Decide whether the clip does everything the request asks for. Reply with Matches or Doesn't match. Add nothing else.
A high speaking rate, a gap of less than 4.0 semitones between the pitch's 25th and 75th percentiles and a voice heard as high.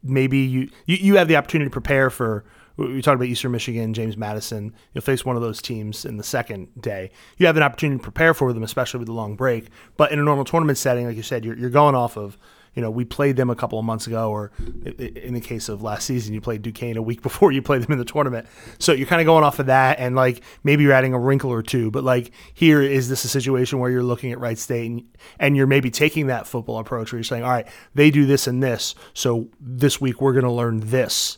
Doesn't match